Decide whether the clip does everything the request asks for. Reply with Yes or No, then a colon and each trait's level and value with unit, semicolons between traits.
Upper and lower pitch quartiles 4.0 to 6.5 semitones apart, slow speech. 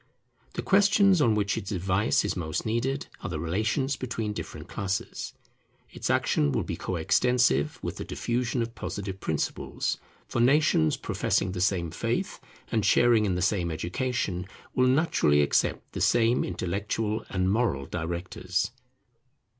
No: average, 5.3 semitones; average, 145 wpm